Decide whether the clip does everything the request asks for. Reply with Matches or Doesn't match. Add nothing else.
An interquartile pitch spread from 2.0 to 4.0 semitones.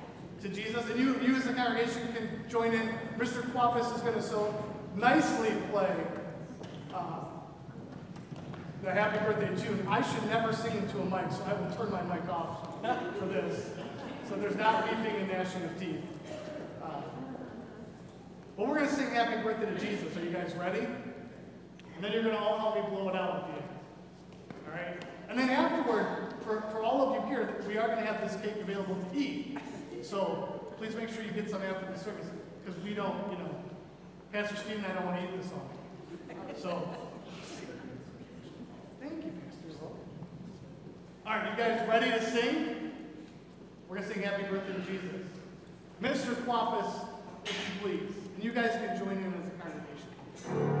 Matches